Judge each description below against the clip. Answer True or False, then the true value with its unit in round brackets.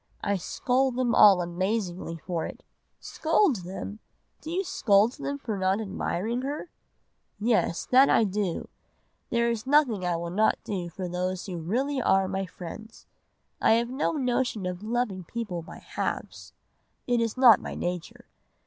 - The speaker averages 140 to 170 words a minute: True (160 wpm)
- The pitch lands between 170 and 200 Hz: False (210 Hz)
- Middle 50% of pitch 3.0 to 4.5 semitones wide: False (5.1 semitones)